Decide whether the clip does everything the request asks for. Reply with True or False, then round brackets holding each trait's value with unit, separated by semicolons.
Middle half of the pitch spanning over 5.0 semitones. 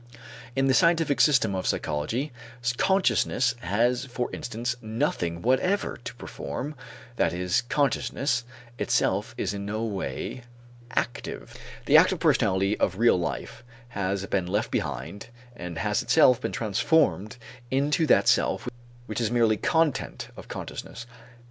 True (5.6 semitones)